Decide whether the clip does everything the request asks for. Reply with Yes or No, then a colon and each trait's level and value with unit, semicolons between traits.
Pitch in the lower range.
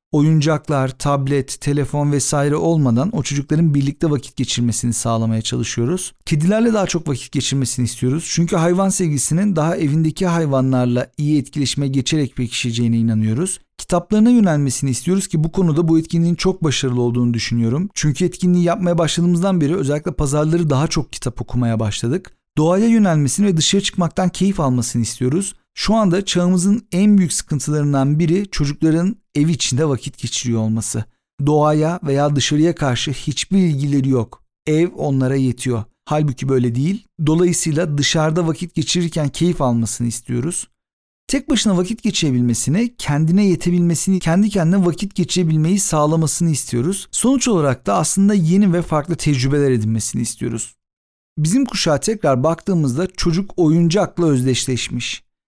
No: medium, 155 Hz